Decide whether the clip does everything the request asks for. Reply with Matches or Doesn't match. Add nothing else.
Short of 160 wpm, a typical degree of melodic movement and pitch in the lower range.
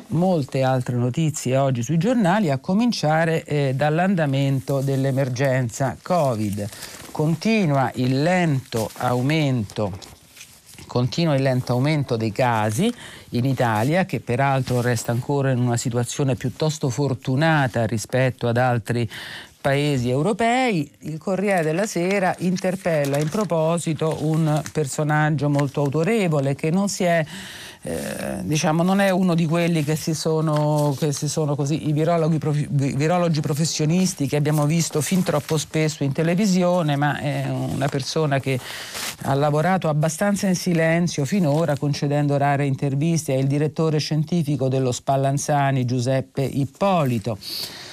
Doesn't match